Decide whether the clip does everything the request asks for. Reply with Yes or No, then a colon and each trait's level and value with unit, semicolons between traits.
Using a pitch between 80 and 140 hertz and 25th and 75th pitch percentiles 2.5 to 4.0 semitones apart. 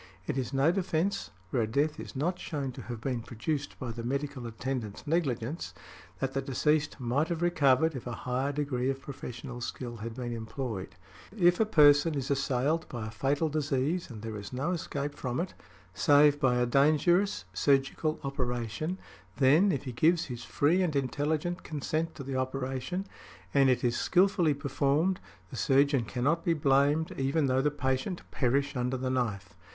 Yes: low, 135 Hz; average, 3.7 semitones